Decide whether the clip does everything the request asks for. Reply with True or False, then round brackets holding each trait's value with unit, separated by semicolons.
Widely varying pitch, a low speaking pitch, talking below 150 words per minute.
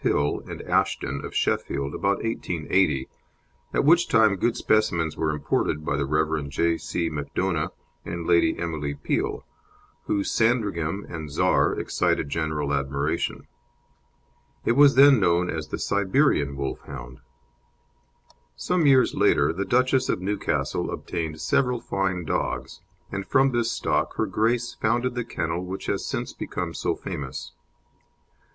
True (7.0 semitones; 85 Hz; 135 wpm)